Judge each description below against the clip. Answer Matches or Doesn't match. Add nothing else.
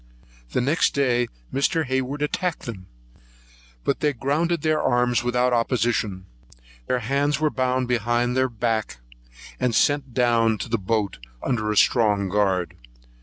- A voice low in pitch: Matches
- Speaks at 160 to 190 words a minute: Doesn't match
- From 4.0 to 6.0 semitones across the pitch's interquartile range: Doesn't match